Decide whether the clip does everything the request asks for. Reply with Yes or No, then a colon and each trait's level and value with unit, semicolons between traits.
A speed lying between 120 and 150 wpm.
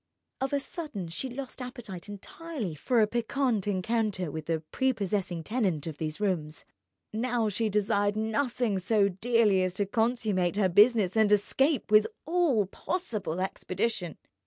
Yes: average, 145 wpm